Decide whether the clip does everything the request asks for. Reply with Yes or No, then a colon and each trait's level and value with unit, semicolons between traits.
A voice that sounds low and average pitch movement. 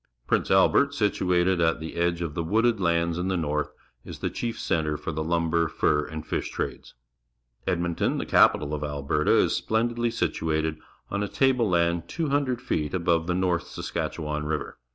Yes: very low, 85 Hz; average, 3.3 semitones